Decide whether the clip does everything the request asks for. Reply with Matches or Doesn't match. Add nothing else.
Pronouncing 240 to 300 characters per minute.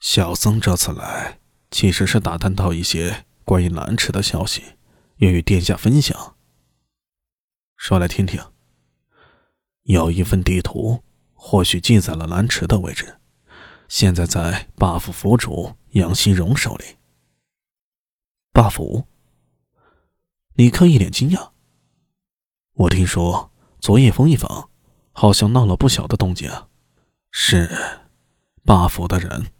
Doesn't match